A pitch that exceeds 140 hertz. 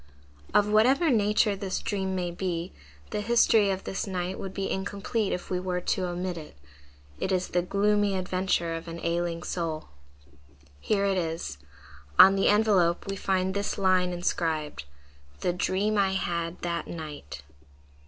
Yes: medium, 185 Hz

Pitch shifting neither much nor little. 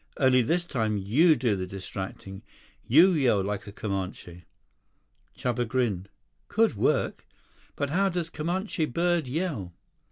No: wide, 8.7 semitones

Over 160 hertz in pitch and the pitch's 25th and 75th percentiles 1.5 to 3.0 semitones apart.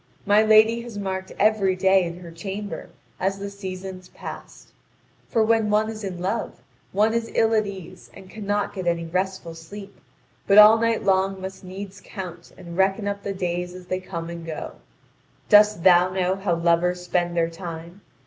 Yes: high, 190 Hz; narrow, 2.5 semitones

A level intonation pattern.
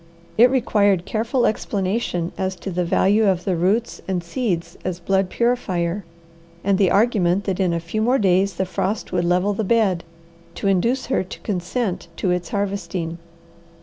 No: average, 3.3 semitones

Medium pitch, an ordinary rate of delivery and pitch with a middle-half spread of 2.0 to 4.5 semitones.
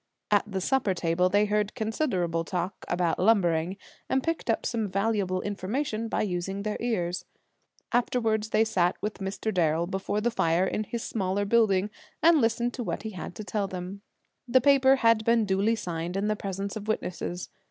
No: high, 205 Hz; average, 180 wpm; average, 3.5 semitones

